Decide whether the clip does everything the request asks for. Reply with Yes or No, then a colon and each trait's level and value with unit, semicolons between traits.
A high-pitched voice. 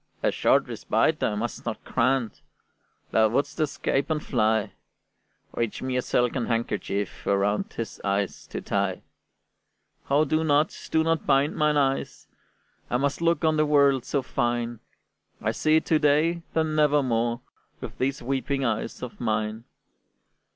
No: low, 135 Hz